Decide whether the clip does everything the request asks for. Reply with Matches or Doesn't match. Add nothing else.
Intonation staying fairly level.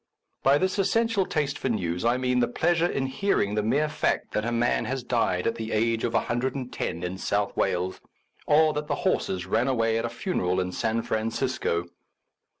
Doesn't match